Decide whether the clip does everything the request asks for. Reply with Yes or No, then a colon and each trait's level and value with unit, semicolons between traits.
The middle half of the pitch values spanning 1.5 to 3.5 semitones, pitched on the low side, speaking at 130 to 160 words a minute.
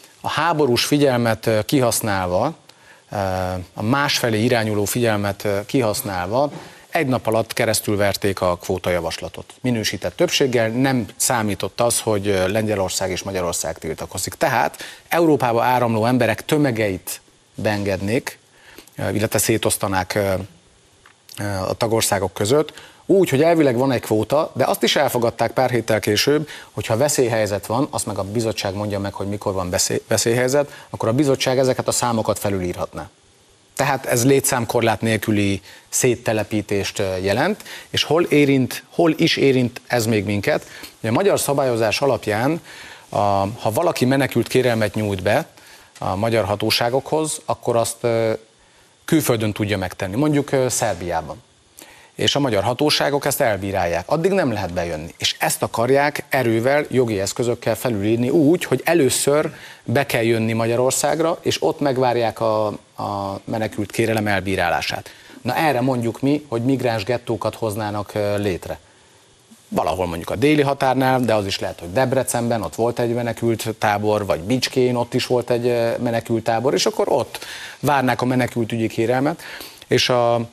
No: average, 3.9 semitones; low, 115 Hz; average, 135 wpm